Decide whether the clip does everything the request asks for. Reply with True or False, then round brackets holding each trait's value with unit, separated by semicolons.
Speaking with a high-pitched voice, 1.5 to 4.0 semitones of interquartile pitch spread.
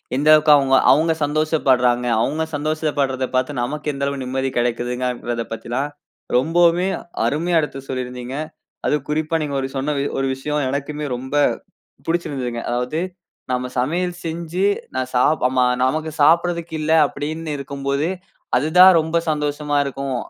False (145 Hz; 3.4 semitones)